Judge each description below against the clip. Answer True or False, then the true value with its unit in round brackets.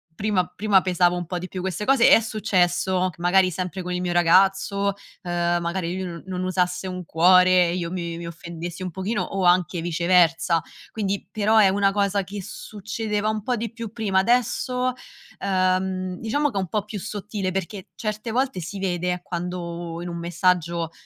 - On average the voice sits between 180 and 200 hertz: True (185 Hz)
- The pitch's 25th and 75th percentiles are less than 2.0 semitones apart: False (2.6 semitones)